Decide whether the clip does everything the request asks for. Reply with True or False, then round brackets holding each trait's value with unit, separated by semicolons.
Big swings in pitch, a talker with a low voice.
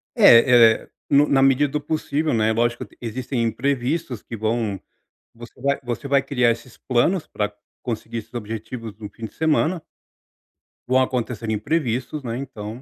False (3.4 semitones; 120 Hz)